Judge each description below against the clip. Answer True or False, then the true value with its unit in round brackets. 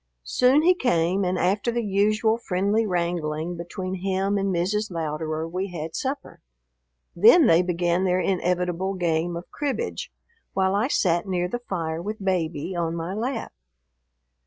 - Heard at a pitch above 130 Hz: True (185 Hz)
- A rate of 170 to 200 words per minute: False (150 wpm)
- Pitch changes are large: False (3.4 semitones)